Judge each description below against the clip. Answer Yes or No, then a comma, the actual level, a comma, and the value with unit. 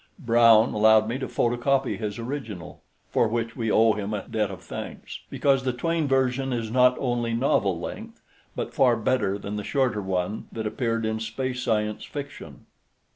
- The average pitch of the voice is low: Yes, low, 115 Hz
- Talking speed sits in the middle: Yes, average, 175 wpm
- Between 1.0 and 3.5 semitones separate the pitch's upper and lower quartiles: Yes, average, 3.1 semitones